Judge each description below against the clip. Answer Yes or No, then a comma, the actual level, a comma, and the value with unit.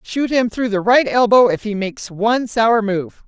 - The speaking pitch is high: Yes, high, 220 Hz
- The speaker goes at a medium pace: No, fast, 220 wpm